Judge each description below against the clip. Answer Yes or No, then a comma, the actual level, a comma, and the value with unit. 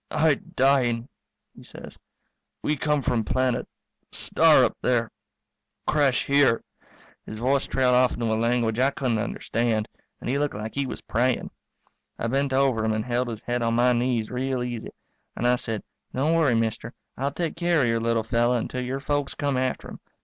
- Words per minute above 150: Yes, average, 185 wpm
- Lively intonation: No, average, 2.8 semitones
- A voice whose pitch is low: Yes, low, 125 Hz